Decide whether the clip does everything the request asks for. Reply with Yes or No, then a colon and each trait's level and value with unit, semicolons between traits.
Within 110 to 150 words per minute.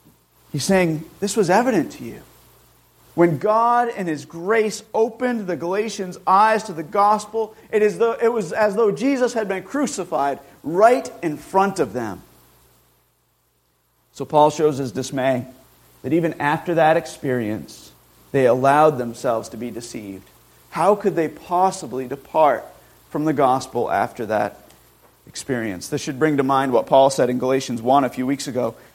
No: average, 160 wpm